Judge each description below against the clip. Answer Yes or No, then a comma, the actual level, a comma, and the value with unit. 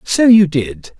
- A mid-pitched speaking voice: Yes, medium, 170 Hz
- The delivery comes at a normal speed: Yes, average, 180 wpm